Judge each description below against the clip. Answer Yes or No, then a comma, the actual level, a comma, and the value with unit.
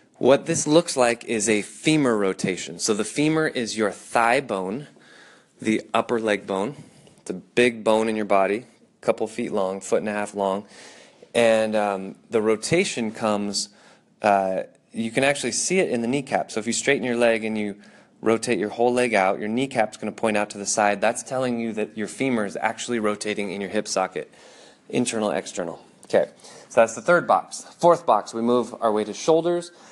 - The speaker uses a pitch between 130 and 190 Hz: No, low, 110 Hz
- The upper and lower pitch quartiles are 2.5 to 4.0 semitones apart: Yes, average, 2.9 semitones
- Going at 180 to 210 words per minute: Yes, average, 200 wpm